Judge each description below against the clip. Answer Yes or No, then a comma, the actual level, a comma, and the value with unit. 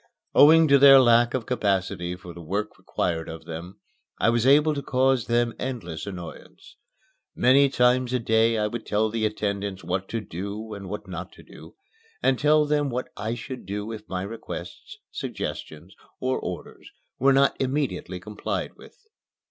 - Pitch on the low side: Yes, low, 110 Hz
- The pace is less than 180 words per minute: Yes, average, 170 wpm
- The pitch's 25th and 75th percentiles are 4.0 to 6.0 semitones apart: Yes, average, 4.9 semitones